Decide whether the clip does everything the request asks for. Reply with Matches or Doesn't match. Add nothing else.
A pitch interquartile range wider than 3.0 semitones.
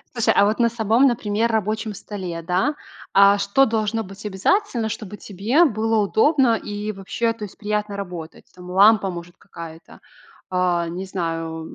Matches